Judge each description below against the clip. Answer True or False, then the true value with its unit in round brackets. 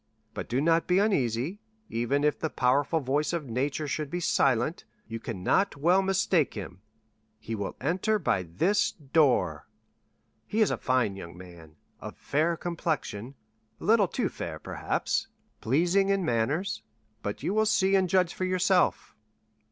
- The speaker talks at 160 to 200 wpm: False (150 wpm)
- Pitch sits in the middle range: True (150 Hz)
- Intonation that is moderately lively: False (8.0 semitones)